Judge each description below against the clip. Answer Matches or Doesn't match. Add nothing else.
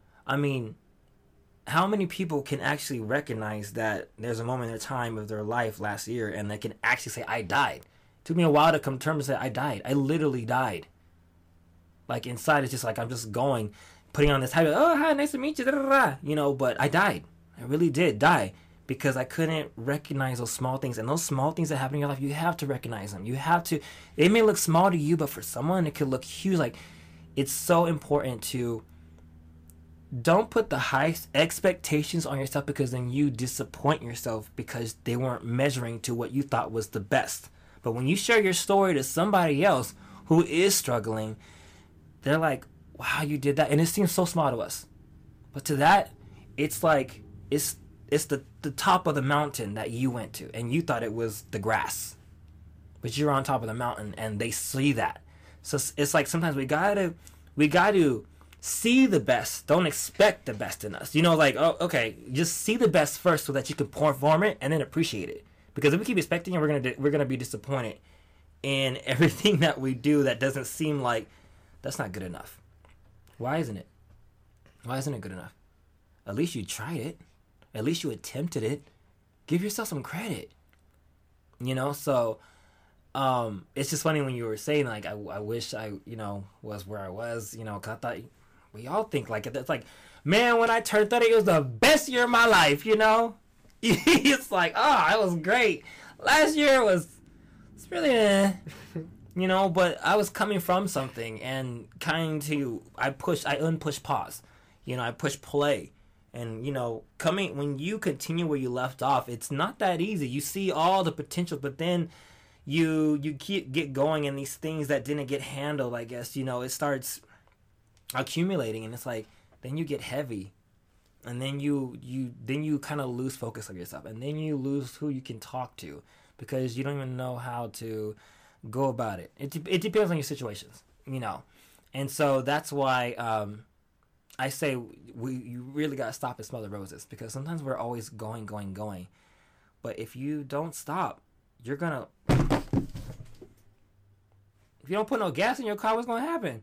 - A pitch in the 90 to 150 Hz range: Matches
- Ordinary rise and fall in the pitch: Doesn't match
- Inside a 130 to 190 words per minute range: Doesn't match